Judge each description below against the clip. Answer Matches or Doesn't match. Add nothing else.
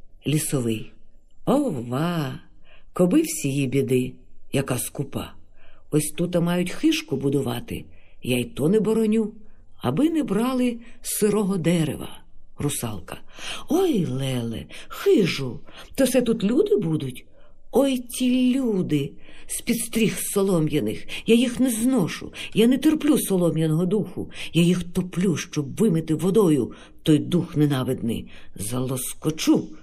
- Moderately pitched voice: Matches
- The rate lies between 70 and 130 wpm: Matches